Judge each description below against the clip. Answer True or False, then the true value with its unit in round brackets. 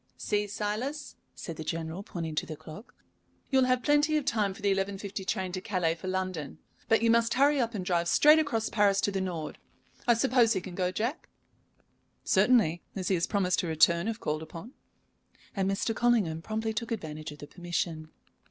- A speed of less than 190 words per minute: False (200 wpm)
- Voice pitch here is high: True (195 Hz)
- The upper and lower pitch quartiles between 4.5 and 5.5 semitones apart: True (5.1 semitones)